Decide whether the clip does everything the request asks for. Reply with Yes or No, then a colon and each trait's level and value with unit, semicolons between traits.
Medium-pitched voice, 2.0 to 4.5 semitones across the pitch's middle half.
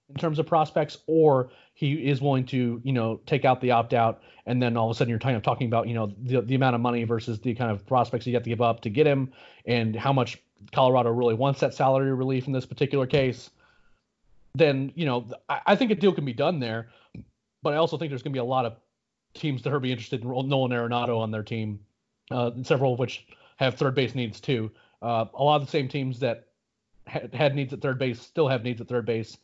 No: low, 130 Hz; average, 3.0 semitones